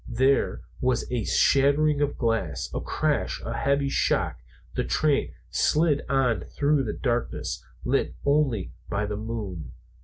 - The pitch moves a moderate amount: Yes, average, 4.3 semitones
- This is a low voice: Yes, low, 130 Hz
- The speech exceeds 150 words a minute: No, average, 145 wpm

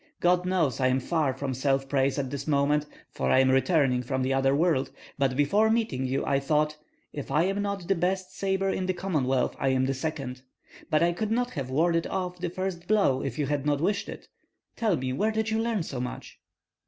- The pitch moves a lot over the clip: Yes, wide, 5.7 semitones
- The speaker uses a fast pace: Yes, fast, 225 wpm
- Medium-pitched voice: Yes, medium, 150 Hz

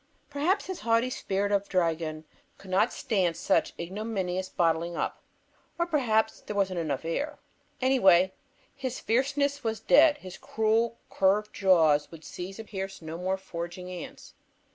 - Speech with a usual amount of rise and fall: Yes, average, 4.7 semitones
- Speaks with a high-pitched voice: Yes, high, 195 Hz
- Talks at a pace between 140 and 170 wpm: Yes, average, 145 wpm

